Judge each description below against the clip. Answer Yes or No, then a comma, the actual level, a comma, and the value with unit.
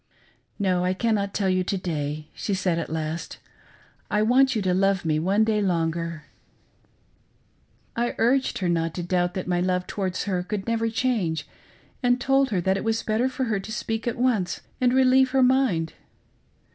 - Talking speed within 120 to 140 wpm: No, average, 185 wpm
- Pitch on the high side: Yes, high, 195 Hz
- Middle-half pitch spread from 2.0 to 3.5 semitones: No, average, 4.8 semitones